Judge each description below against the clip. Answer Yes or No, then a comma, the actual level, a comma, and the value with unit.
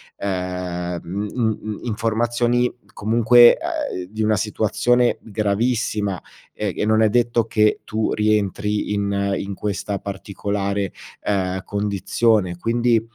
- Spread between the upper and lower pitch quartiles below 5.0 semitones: Yes, narrow, 2.5 semitones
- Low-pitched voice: Yes, low, 105 Hz